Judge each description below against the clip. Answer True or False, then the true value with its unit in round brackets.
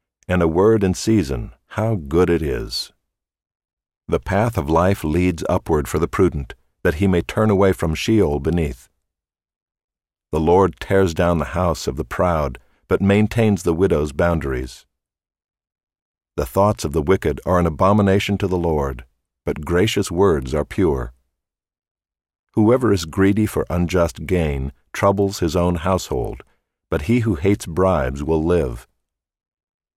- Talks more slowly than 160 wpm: True (145 wpm)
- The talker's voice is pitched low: True (90 Hz)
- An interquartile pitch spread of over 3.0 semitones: True (4.3 semitones)